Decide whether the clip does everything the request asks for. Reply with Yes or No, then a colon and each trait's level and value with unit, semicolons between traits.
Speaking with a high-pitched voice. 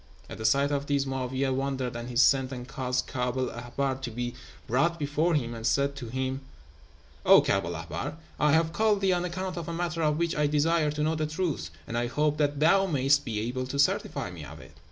No: medium, 140 Hz